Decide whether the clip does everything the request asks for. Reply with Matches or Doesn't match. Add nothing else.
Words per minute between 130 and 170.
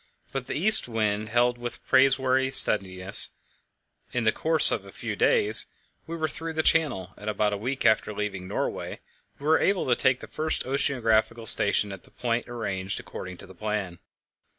Doesn't match